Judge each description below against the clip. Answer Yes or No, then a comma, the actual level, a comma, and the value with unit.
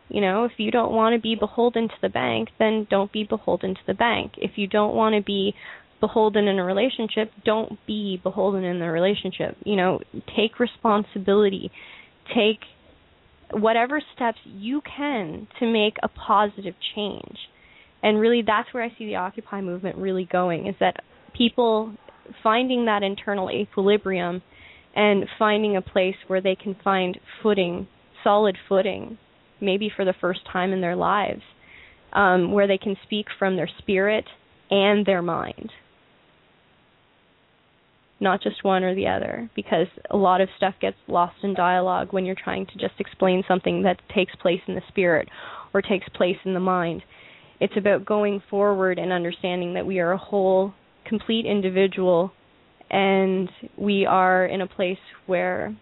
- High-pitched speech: Yes, high, 195 Hz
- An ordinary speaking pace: Yes, average, 160 wpm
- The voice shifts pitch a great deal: No, narrow, 2.5 semitones